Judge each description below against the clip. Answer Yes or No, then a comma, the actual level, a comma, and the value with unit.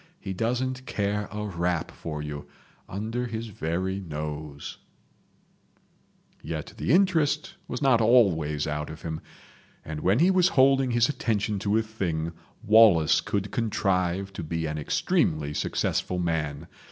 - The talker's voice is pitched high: No, low, 100 Hz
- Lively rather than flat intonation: Yes, wide, 6.4 semitones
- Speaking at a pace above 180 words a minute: No, average, 140 wpm